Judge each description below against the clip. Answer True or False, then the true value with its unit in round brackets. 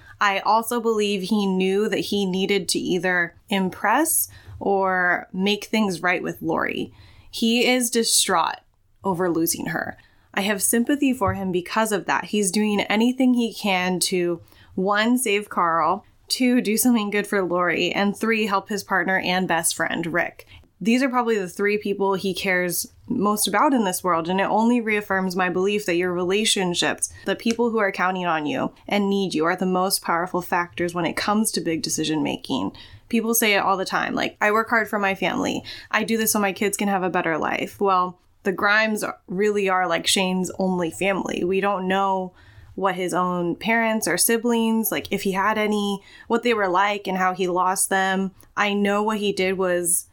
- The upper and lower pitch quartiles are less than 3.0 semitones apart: True (2.6 semitones)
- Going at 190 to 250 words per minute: True (195 wpm)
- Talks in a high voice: True (195 Hz)